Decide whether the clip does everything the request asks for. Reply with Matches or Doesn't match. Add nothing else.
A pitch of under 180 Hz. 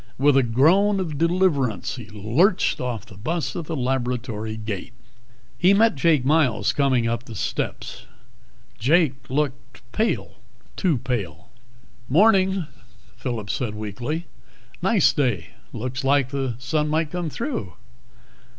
Matches